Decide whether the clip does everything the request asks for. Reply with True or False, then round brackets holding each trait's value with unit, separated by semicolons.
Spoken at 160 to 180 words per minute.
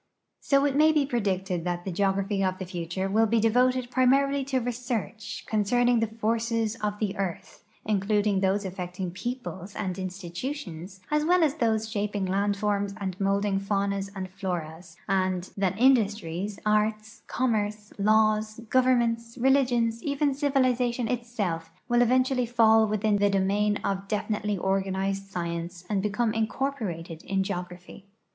False (145 wpm)